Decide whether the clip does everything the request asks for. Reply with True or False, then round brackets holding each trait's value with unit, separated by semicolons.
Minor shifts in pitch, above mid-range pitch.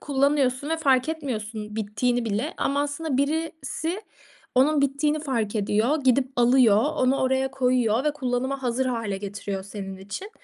False (4.5 semitones; 260 Hz)